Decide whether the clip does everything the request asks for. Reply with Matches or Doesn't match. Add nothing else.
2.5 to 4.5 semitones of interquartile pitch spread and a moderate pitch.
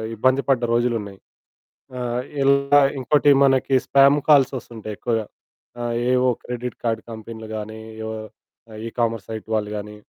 Doesn't match